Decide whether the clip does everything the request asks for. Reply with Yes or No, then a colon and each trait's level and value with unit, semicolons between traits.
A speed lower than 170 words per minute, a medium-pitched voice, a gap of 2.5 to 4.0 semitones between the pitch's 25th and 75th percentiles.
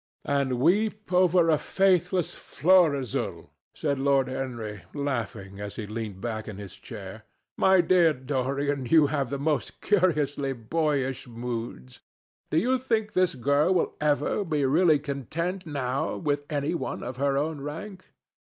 No: average, 145 wpm; medium, 145 Hz; average, 4.9 semitones